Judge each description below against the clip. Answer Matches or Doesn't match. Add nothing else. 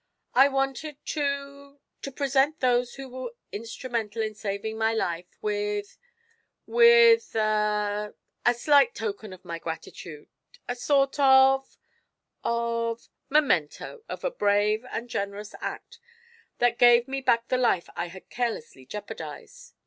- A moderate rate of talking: Doesn't match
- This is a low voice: Doesn't match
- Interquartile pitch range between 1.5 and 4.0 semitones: Doesn't match